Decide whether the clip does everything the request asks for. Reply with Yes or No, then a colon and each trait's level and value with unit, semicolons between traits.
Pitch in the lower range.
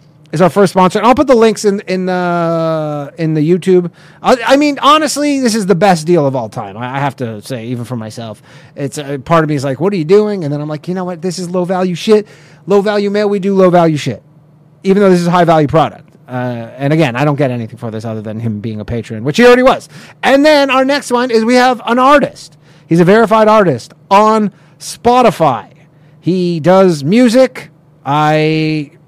No: medium, 170 Hz